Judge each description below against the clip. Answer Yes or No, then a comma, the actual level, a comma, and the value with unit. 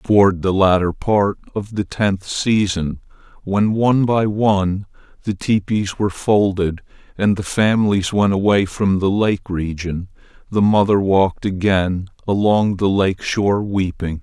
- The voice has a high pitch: No, low, 100 Hz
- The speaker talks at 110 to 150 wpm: Yes, average, 145 wpm